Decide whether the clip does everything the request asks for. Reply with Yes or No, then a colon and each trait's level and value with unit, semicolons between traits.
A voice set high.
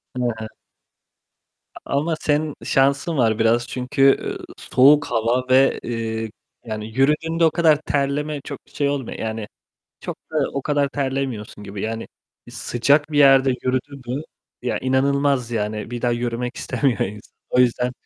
No: low, 130 Hz